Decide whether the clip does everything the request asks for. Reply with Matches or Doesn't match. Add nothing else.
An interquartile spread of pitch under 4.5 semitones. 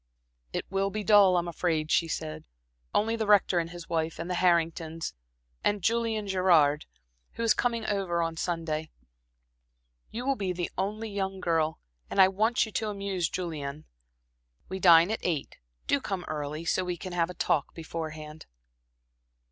Matches